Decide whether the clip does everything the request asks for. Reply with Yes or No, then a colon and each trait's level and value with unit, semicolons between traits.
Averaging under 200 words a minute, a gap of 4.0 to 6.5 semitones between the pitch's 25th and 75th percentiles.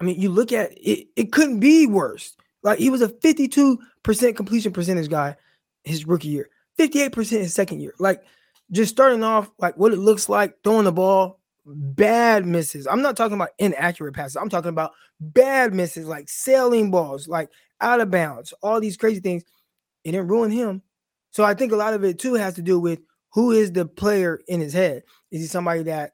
No: fast, 205 wpm; average, 4.7 semitones